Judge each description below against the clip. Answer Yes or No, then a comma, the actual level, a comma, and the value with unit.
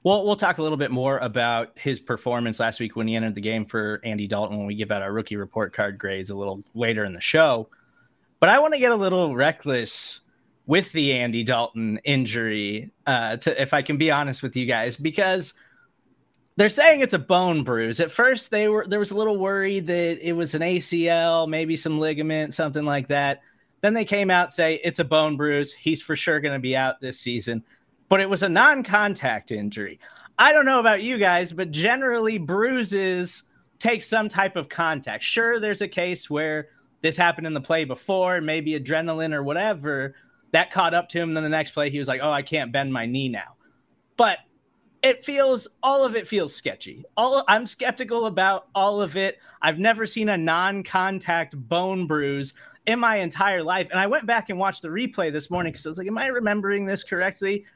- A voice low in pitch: No, medium, 165 Hz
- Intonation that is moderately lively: No, wide, 6.5 semitones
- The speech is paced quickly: Yes, fast, 210 wpm